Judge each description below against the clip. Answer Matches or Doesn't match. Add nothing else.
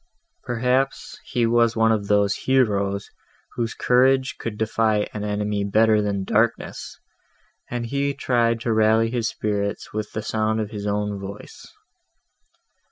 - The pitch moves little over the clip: Matches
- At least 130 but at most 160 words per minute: Matches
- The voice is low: Matches